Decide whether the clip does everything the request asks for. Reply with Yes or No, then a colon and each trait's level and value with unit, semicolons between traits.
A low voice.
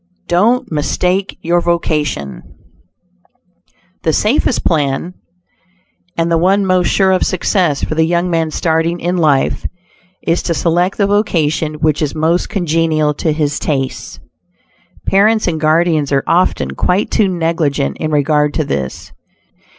No: medium, 165 Hz